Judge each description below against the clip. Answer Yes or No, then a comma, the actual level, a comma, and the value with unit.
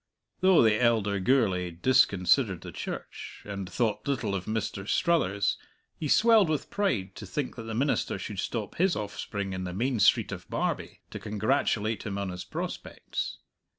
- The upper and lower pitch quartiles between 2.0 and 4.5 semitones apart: No, average, 5.2 semitones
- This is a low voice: Yes, low, 110 Hz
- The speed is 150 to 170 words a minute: Yes, average, 165 wpm